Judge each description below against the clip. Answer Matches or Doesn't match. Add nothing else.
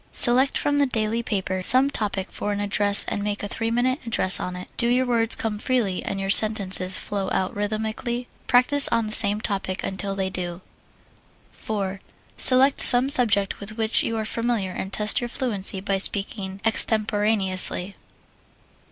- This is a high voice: Matches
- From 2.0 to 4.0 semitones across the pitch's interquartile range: Matches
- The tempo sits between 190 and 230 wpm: Doesn't match